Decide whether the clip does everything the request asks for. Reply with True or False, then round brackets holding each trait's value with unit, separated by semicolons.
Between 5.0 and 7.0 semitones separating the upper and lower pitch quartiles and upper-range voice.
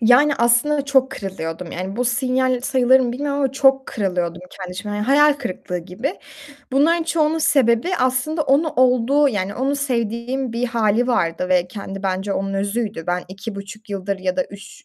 True (5.4 semitones; 235 Hz)